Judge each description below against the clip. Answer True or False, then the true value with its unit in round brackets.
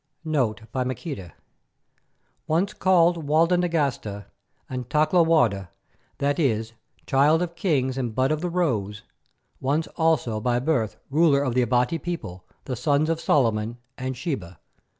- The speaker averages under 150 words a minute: True (140 wpm)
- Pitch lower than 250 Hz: True (135 Hz)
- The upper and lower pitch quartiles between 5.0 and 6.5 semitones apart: True (5.4 semitones)